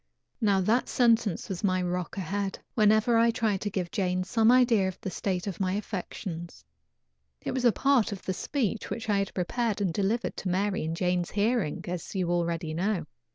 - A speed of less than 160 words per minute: No, average, 195 wpm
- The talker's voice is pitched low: No, high, 195 Hz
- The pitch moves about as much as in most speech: Yes, average, 3.6 semitones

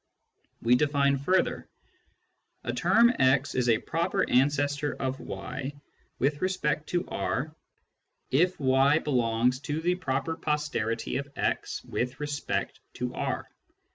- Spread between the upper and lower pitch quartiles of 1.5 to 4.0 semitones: Yes, average, 2.9 semitones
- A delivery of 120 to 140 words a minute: Yes, slow, 135 wpm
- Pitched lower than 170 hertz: Yes, medium, 140 Hz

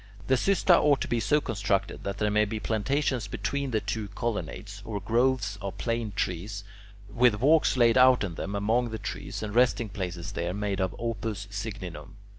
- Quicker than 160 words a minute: Yes, average, 185 wpm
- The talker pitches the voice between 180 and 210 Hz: No, low, 105 Hz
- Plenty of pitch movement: No, average, 3.2 semitones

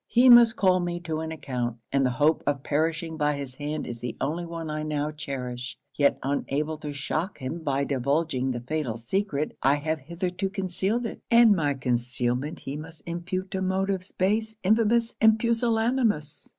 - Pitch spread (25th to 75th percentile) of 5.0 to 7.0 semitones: Yes, average, 5.3 semitones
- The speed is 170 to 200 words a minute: Yes, average, 175 wpm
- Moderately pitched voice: Yes, medium, 155 Hz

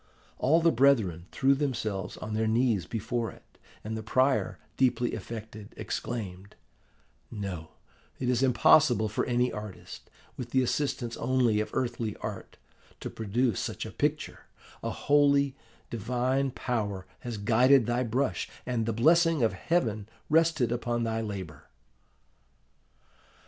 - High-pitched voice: No, low, 120 Hz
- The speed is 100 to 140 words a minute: Yes, slow, 135 wpm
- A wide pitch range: No, average, 3.3 semitones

